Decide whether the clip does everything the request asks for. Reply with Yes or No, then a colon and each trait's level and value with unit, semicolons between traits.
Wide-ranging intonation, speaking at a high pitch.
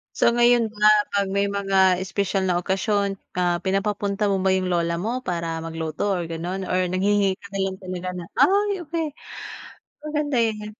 No: narrow, 2.6 semitones; high, 195 Hz